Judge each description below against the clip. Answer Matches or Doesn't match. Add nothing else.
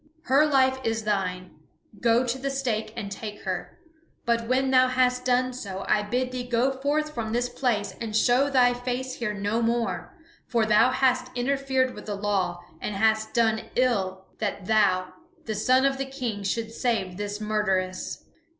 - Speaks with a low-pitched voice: Doesn't match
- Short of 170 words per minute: Doesn't match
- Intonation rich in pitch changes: Doesn't match